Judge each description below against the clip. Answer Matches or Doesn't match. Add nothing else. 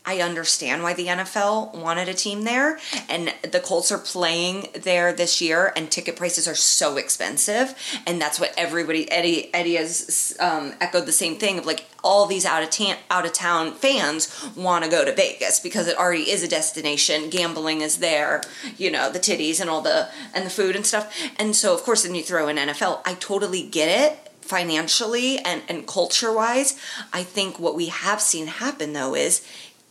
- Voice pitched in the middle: Matches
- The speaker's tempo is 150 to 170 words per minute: Doesn't match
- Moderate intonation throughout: Matches